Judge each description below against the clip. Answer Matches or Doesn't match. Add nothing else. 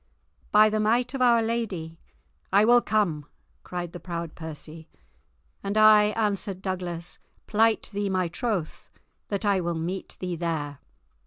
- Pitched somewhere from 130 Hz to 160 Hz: Doesn't match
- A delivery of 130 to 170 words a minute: Matches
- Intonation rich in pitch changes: Doesn't match